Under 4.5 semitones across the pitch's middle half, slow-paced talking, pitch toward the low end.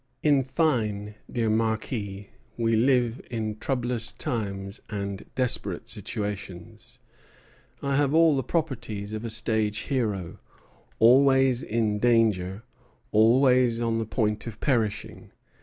Yes: average, 3.3 semitones; slow, 115 wpm; low, 115 Hz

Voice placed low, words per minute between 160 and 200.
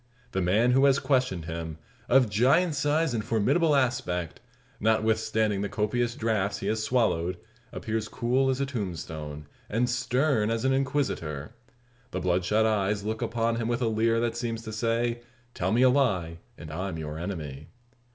Yes: low, 110 Hz; average, 165 wpm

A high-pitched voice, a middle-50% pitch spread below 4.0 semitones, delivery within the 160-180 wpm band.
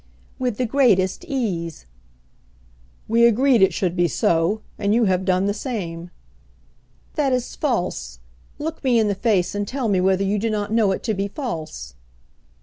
No: high, 205 Hz; average, 4.6 semitones; average, 170 wpm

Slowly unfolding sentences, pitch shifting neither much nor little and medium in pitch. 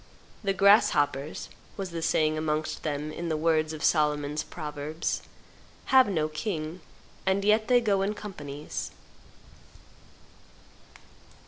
Yes: slow, 115 wpm; average, 4.4 semitones; medium, 155 Hz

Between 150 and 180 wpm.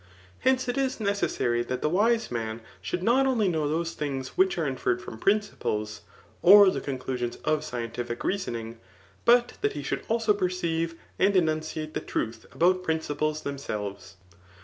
Yes: average, 165 wpm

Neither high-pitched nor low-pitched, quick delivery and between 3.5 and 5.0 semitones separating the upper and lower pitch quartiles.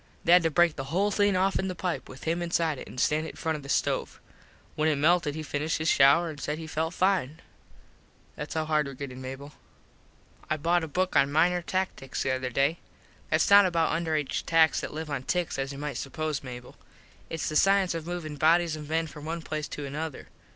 No: medium, 155 Hz; fast, 225 wpm; average, 3.0 semitones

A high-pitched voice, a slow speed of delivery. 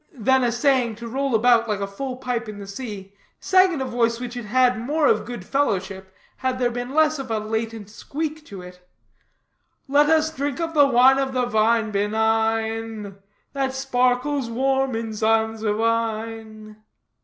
No: high, 235 Hz; average, 165 wpm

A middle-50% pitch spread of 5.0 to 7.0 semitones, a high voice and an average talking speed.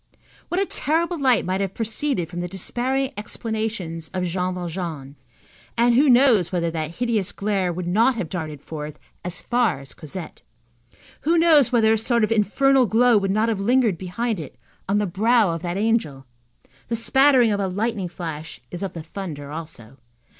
Yes: wide, 5.5 semitones; high, 200 Hz; average, 180 wpm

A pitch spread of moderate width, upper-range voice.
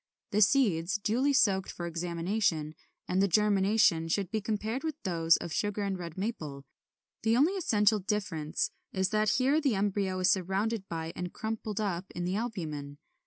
Yes: average, 4.0 semitones; high, 195 Hz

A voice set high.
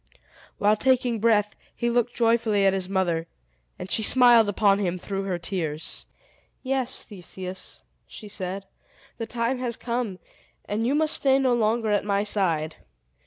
Yes: high, 210 Hz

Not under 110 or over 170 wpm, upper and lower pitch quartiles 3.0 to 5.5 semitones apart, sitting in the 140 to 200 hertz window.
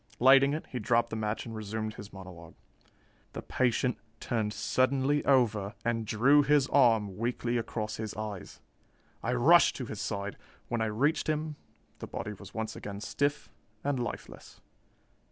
No: average, 155 wpm; average, 3.9 semitones; low, 115 Hz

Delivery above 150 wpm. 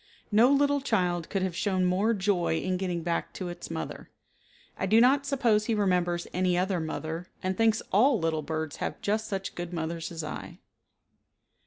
Yes: average, 180 wpm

